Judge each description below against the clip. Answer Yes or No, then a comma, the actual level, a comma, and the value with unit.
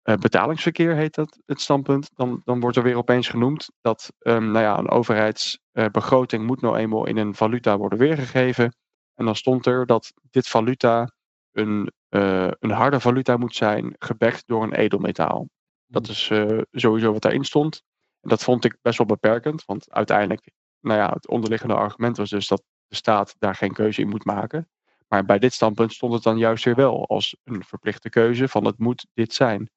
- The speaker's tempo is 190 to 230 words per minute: Yes, average, 195 wpm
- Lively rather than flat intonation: No, average, 2.7 semitones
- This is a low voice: Yes, low, 115 Hz